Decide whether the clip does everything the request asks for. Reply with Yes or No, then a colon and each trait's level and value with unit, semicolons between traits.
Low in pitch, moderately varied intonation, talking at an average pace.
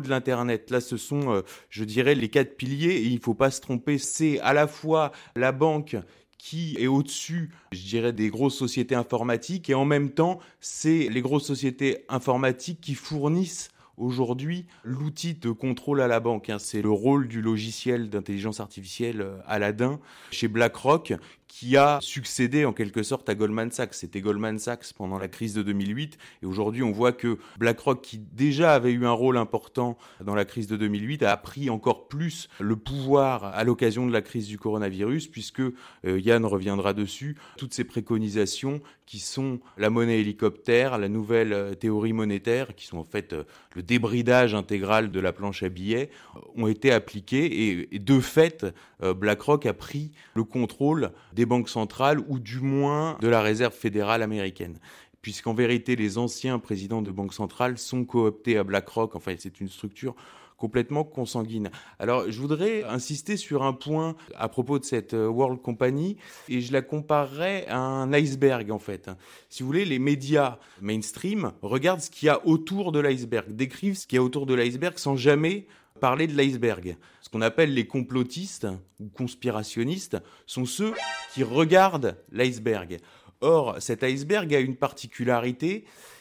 Yes: low, 125 Hz; average, 4.5 semitones; average, 175 wpm